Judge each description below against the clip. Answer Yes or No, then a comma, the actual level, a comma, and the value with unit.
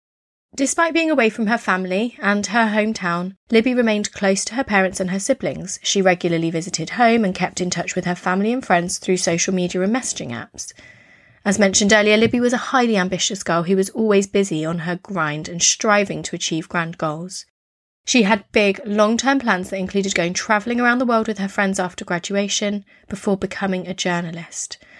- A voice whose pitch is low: No, high, 195 Hz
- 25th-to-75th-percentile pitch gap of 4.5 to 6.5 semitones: No, average, 3.5 semitones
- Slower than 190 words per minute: No, average, 195 wpm